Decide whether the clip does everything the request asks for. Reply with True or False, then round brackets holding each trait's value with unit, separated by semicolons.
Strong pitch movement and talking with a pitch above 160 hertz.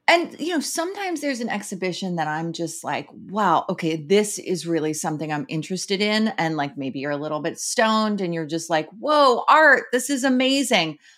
True (7.6 semitones; 190 Hz)